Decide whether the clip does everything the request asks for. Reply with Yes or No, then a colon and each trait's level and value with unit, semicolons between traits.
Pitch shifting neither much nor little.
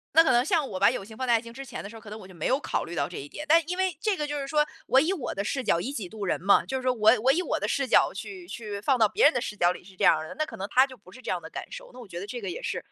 No: wide, 6.5 semitones